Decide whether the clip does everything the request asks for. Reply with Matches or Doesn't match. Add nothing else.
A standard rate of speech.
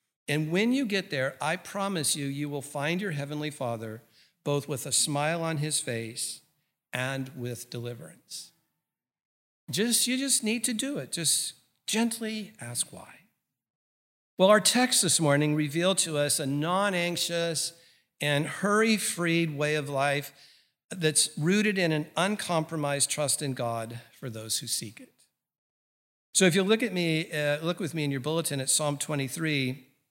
Matches